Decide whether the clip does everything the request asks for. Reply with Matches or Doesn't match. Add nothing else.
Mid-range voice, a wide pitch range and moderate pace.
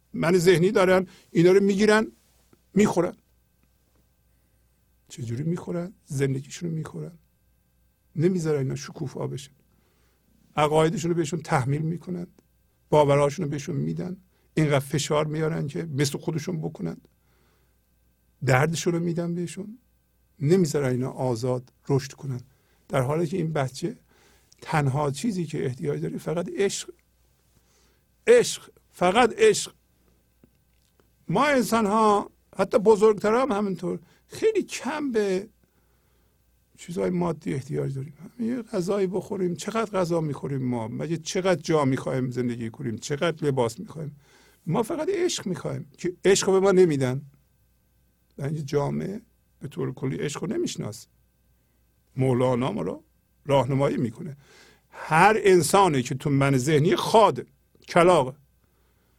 Matches